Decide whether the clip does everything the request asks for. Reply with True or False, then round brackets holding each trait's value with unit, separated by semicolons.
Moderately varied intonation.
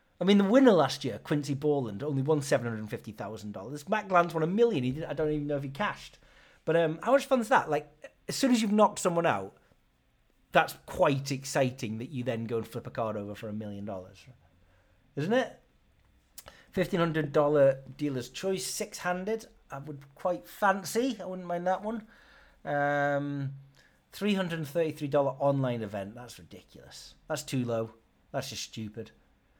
False (7.3 semitones)